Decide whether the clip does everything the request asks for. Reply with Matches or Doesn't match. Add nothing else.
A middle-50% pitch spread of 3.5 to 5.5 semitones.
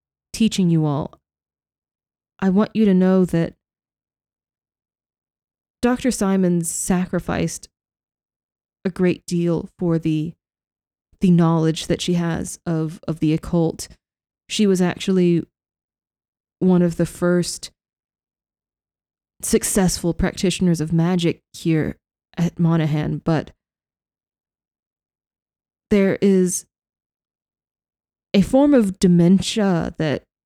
Doesn't match